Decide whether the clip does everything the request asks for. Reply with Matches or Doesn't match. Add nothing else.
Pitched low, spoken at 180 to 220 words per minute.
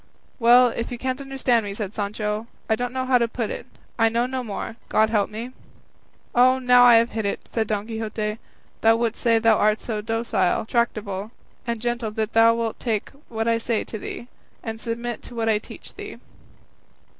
Doesn't match